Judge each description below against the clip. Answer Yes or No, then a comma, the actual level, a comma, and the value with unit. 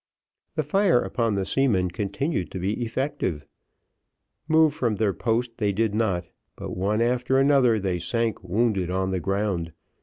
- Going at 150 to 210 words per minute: Yes, average, 155 wpm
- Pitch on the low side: Yes, low, 110 Hz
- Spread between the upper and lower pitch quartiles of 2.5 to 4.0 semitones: No, average, 4.6 semitones